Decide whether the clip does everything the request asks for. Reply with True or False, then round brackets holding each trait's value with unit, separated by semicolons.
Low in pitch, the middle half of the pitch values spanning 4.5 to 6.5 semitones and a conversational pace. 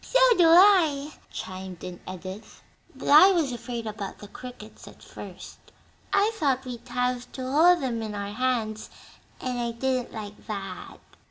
False (245 Hz; 4.9 semitones; 160 wpm)